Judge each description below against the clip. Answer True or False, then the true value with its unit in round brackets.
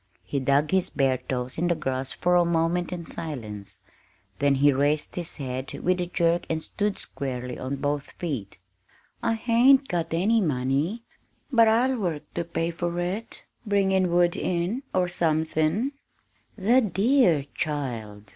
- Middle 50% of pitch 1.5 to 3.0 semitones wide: False (5.1 semitones)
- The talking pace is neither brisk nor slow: True (155 wpm)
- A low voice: False (170 Hz)